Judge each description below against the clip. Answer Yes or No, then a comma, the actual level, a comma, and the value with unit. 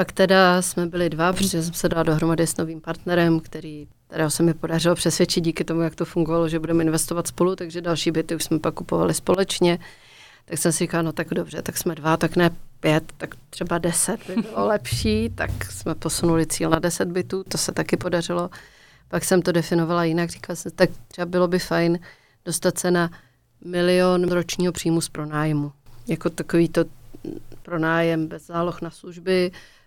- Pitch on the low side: No, medium, 170 Hz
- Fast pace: Yes, fast, 190 wpm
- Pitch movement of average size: No, narrow, 1.5 semitones